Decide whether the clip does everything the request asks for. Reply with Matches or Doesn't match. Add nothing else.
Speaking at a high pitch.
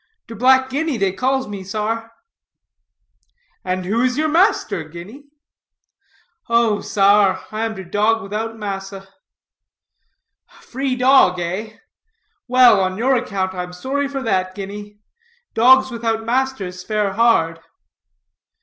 Matches